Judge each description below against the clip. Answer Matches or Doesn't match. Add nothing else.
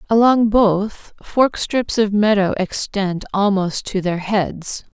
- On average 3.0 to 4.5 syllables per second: Matches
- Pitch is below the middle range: Doesn't match